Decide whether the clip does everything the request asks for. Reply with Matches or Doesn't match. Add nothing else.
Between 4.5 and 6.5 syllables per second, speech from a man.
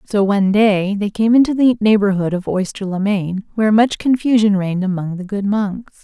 Doesn't match